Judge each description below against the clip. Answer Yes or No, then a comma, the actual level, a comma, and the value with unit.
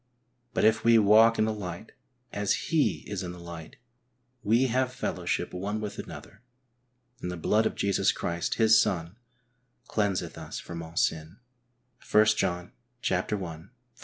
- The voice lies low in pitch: Yes, low, 100 Hz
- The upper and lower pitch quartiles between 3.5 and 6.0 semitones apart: Yes, average, 4.1 semitones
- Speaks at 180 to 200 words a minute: No, average, 155 wpm